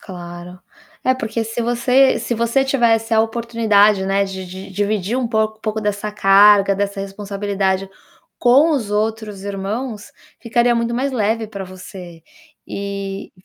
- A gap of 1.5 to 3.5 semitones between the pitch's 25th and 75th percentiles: Yes, average, 2.9 semitones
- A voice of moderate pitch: No, high, 210 Hz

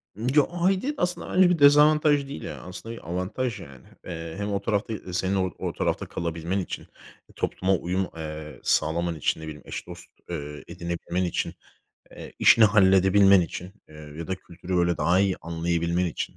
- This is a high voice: No, very low, 95 Hz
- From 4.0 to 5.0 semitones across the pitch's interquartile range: Yes, average, 4.4 semitones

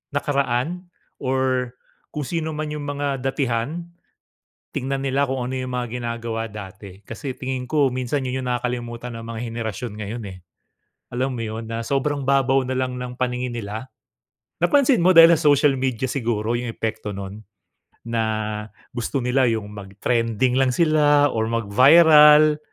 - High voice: No, low, 125 Hz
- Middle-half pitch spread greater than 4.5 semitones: No, average, 3.5 semitones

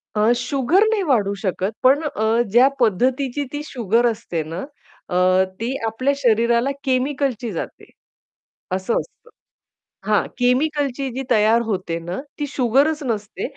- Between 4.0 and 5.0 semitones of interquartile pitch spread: Yes, average, 4.3 semitones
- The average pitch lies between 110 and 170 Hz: No, high, 240 Hz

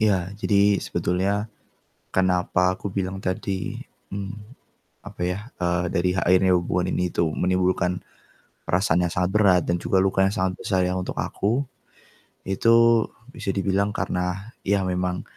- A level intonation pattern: Yes, narrow, 1.8 semitones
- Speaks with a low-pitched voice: Yes, very low, 95 Hz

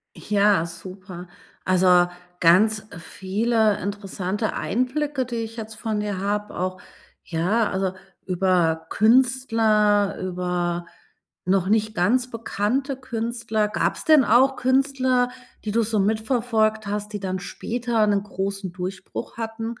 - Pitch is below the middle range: No, high, 210 Hz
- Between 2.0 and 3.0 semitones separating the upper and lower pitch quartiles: No, average, 3.6 semitones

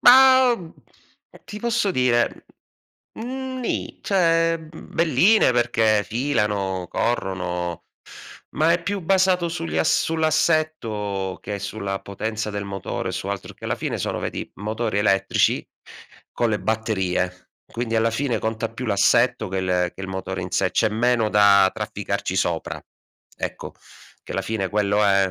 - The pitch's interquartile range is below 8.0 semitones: No, wide, 8.5 semitones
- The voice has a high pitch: No, low, 110 Hz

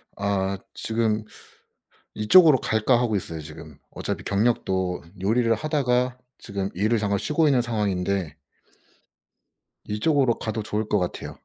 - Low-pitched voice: Yes, low, 105 Hz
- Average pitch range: Yes, average, 3.8 semitones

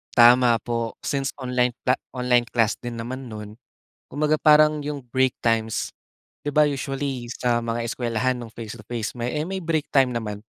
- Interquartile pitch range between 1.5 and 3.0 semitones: Yes, average, 2.7 semitones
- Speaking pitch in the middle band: No, low, 125 Hz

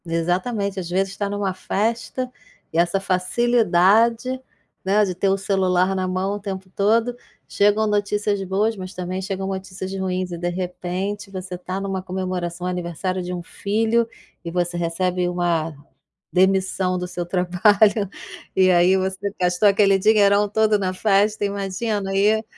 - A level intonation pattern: Yes, narrow, 2.0 semitones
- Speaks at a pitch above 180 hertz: Yes, high, 190 Hz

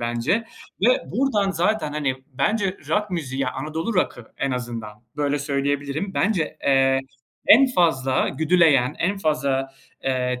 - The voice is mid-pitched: Yes, medium, 145 Hz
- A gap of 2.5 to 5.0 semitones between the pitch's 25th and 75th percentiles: No, wide, 5.6 semitones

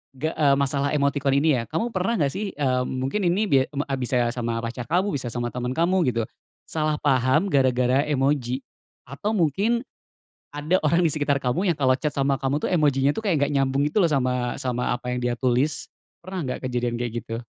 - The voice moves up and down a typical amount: Yes, average, 3.8 semitones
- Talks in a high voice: No, medium, 140 Hz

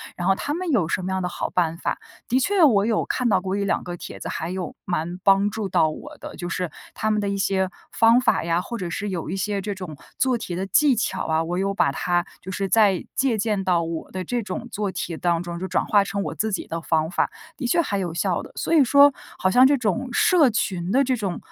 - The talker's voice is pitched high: Yes, high, 195 Hz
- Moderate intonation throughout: Yes, average, 4.2 semitones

